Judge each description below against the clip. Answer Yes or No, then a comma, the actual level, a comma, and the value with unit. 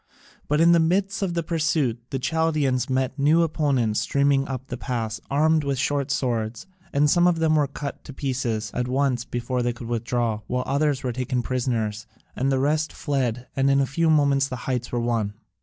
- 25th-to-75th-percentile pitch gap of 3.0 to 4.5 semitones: Yes, average, 3.4 semitones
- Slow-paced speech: No, average, 200 wpm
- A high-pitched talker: No, low, 135 Hz